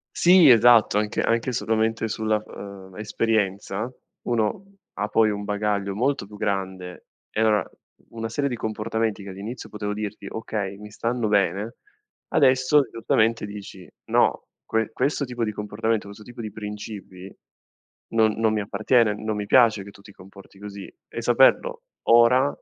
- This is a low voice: Yes, low, 110 Hz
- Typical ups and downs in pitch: No, narrow, 2.1 semitones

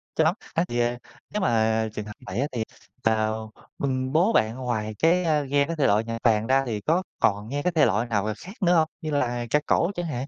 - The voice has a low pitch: Yes, low, 125 Hz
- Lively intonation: Yes, wide, 6.1 semitones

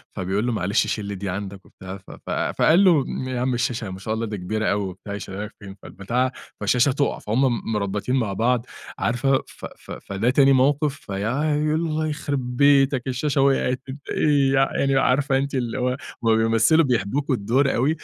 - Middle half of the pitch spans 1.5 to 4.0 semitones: No, average, 4.6 semitones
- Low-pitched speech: Yes, low, 125 Hz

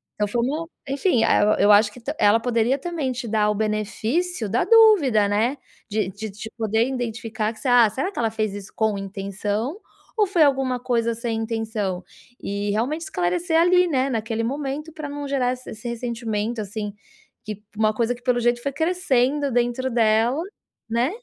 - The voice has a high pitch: Yes, high, 235 Hz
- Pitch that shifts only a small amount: No, average, 4.0 semitones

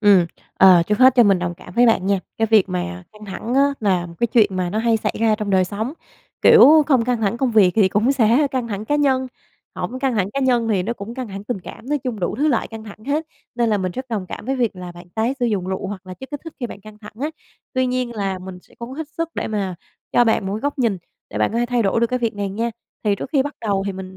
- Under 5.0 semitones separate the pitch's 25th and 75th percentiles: Yes, average, 4.5 semitones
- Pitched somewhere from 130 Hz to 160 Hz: No, high, 220 Hz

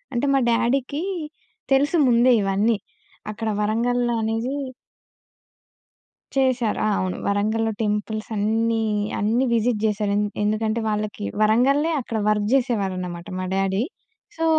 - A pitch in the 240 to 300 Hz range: No, high, 225 Hz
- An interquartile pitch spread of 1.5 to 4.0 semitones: Yes, average, 2.7 semitones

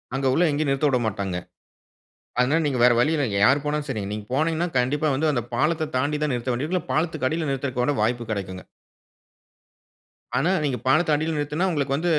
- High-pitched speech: No, medium, 140 Hz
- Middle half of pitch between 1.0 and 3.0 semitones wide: No, average, 3.8 semitones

